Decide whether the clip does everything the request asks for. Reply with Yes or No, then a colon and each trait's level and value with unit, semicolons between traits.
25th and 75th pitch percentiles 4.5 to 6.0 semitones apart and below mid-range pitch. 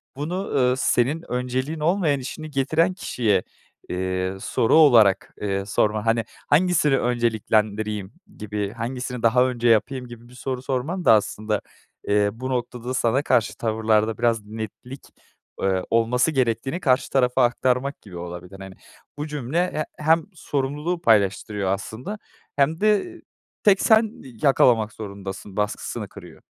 Yes: average, 5.0 semitones; low, 125 Hz